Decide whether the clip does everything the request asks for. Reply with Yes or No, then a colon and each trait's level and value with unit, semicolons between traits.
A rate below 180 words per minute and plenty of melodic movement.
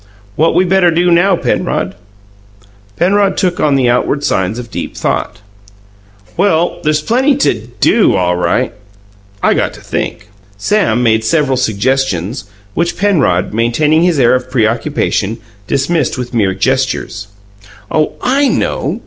Yes: average, 140 wpm; wide, 7.4 semitones